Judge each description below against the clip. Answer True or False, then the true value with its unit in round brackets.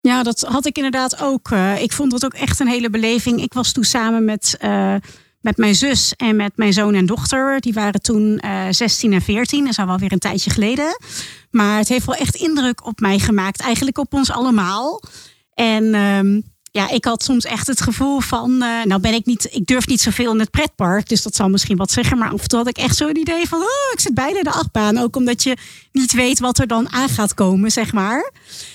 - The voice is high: True (230 Hz)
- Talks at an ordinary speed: False (240 wpm)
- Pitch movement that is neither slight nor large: True (3.5 semitones)